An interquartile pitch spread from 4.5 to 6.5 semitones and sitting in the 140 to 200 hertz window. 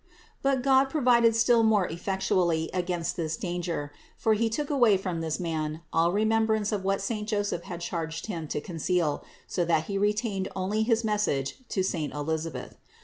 Yes: average, 4.8 semitones; high, 190 Hz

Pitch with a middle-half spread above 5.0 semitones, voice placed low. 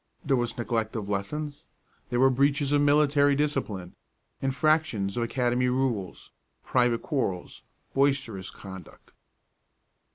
No: average, 4.4 semitones; low, 125 Hz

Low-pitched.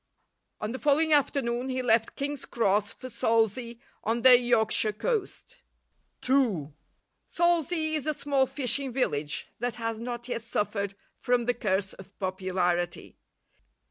No: high, 240 Hz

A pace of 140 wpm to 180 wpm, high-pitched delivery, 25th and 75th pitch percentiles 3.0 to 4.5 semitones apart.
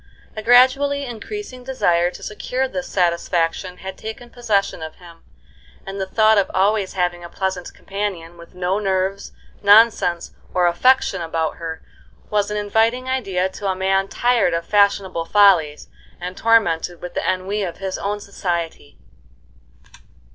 Yes: average, 145 wpm; high, 195 Hz; average, 3.8 semitones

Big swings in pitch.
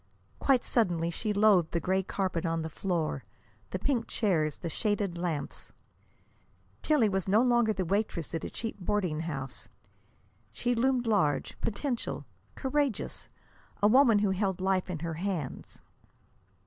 No: average, 4.9 semitones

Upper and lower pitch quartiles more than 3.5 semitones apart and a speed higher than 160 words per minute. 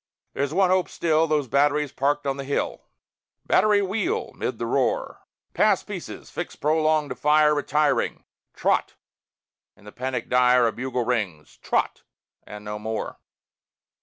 No: average, 4.2 semitones; average, 145 wpm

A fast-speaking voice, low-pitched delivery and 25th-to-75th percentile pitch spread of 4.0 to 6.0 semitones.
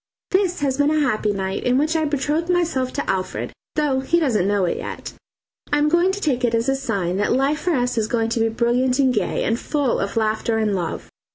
No: fast, 240 wpm; very high, 255 Hz; average, 5.0 semitones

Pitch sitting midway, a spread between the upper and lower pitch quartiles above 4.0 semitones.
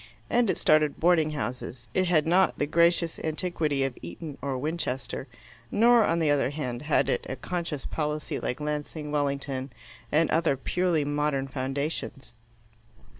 No: medium, 150 Hz; average, 3.3 semitones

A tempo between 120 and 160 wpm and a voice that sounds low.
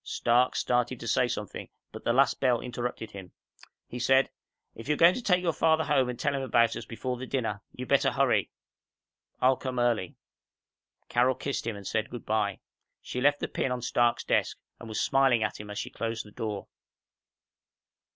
No: average, 195 wpm; low, 120 Hz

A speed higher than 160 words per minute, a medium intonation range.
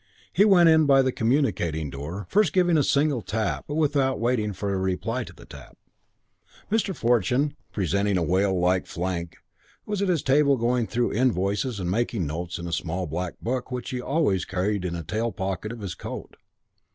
No: average, 190 wpm; wide, 6.9 semitones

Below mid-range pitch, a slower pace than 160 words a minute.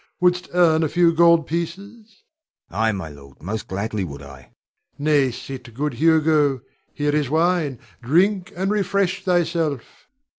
No: medium, 155 Hz; average, 150 wpm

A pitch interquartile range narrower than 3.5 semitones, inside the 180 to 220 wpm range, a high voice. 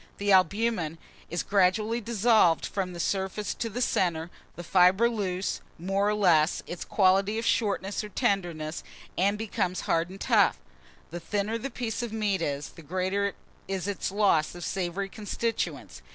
No: average, 3.1 semitones; average, 160 wpm; high, 195 Hz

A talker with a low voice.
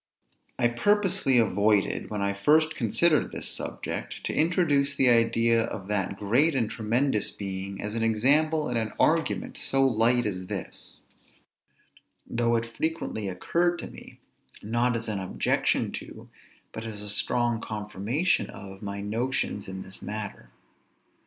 Yes: low, 115 Hz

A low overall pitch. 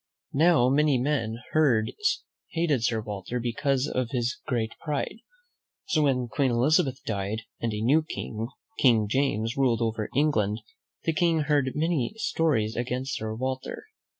Yes: low, 130 Hz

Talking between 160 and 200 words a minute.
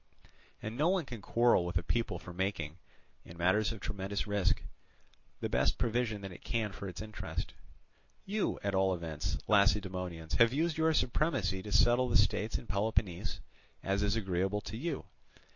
Yes: average, 170 wpm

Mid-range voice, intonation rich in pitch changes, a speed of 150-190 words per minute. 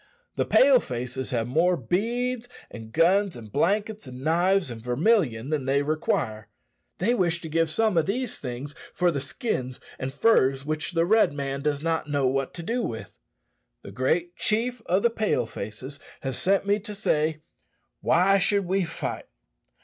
Yes: medium, 165 Hz; wide, 7.0 semitones; average, 170 wpm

